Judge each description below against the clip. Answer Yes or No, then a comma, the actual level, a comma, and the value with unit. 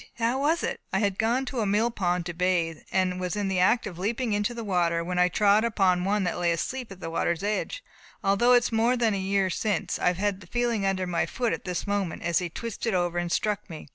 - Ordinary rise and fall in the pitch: Yes, average, 4.0 semitones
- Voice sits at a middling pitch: No, high, 195 Hz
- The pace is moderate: No, fast, 255 wpm